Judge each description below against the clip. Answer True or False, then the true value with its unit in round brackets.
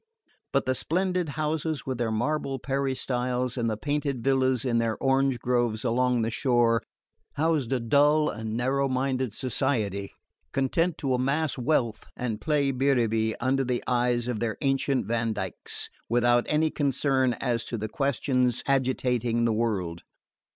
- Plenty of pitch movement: False (2.8 semitones)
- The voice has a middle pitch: False (125 Hz)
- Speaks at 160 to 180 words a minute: False (145 wpm)